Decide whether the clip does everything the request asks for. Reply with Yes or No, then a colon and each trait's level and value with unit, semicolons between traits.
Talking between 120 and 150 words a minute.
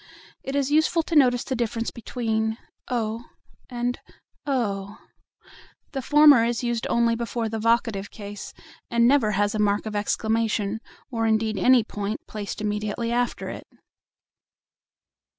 Yes: slow, 135 wpm